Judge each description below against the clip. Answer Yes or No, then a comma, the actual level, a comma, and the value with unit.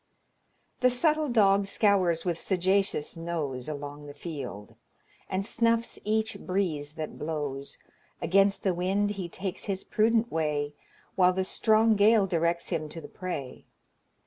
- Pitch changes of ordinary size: Yes, average, 4.8 semitones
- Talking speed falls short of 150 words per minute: Yes, average, 140 wpm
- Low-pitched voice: No, medium, 185 Hz